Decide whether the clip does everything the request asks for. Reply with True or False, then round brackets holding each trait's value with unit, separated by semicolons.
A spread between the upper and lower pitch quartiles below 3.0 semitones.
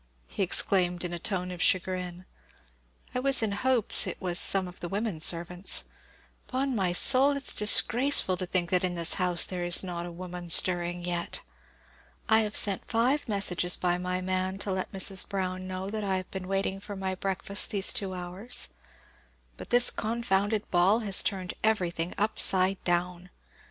True (2.6 semitones)